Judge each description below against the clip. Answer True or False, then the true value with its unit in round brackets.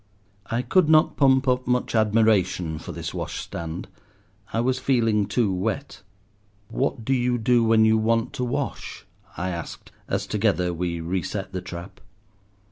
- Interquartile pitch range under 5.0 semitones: False (5.3 semitones)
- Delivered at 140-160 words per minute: True (150 wpm)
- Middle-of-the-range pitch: False (110 Hz)